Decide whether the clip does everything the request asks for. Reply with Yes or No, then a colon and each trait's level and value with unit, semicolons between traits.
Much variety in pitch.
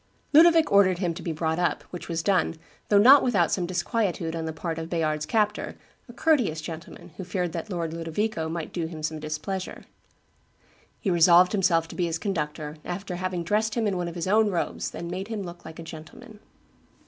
No: average, 3.6 semitones